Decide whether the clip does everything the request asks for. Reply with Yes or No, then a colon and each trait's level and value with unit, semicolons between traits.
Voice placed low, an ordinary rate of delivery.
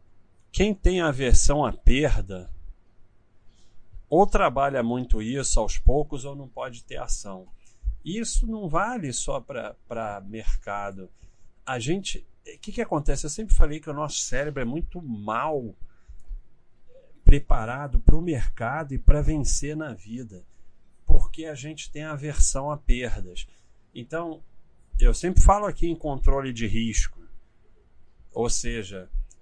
Yes: low, 125 Hz; average, 135 wpm